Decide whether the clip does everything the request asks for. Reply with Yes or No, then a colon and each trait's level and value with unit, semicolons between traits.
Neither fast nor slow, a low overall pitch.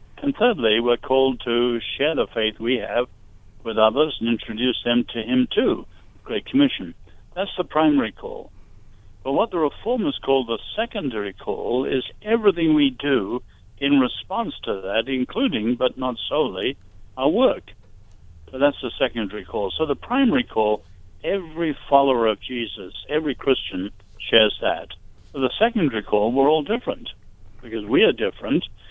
Yes: average, 155 wpm; low, 120 Hz